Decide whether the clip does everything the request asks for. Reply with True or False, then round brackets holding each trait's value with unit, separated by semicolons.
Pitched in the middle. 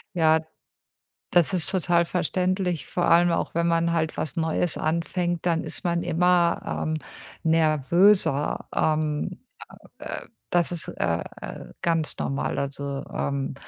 True (165 Hz)